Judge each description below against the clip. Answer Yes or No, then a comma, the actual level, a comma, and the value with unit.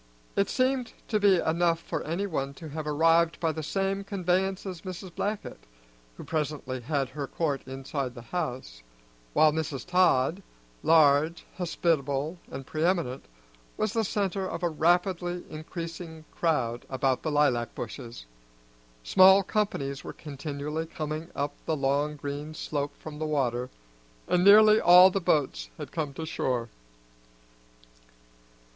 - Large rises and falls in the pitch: No, average, 4.1 semitones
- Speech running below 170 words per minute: Yes, average, 140 wpm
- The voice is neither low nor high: Yes, medium, 160 Hz